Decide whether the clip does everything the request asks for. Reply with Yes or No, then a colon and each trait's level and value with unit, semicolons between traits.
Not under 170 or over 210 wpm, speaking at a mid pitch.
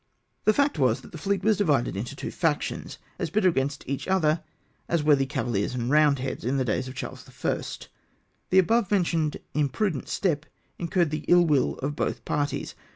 Yes: average, 185 wpm; medium, 150 Hz